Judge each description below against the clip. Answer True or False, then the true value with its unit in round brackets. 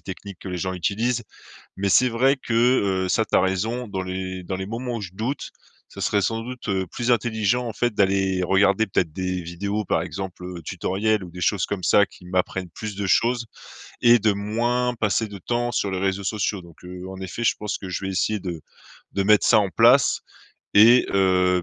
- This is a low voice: True (100 Hz)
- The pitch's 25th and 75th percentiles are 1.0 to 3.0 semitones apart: False (3.6 semitones)